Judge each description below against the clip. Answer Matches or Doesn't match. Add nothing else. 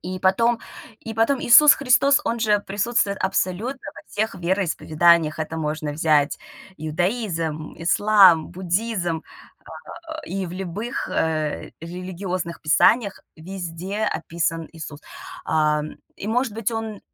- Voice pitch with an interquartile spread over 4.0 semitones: Matches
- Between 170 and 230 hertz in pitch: Matches